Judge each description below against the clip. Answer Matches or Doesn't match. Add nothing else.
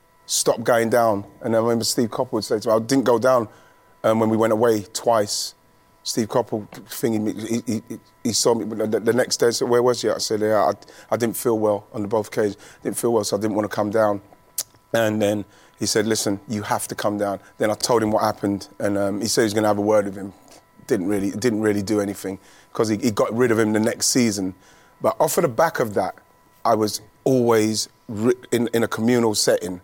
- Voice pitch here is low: Matches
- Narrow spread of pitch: Matches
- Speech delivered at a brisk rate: Matches